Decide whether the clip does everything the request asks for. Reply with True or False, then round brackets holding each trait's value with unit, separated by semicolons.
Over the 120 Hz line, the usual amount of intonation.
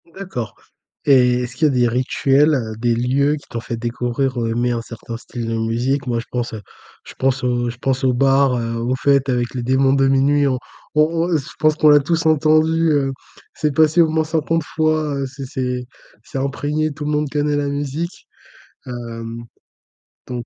True (135 Hz; 3.5 semitones)